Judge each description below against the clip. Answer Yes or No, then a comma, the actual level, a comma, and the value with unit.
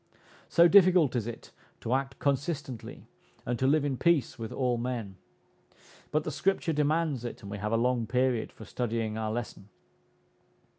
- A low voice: Yes, low, 125 Hz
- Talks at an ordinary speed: Yes, average, 165 wpm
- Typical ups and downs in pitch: Yes, average, 4.4 semitones